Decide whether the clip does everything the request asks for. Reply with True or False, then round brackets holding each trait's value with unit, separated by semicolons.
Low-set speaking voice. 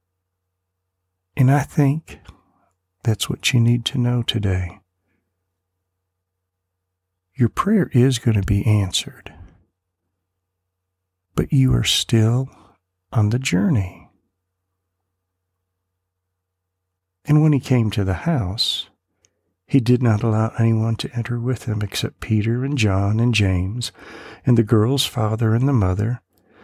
True (100 Hz)